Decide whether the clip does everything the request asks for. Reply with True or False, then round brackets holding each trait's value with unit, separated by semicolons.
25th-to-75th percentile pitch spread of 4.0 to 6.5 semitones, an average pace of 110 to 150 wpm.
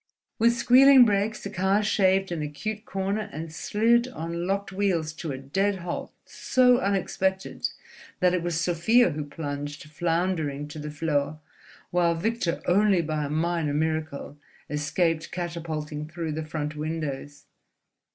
True (4.3 semitones; 140 wpm)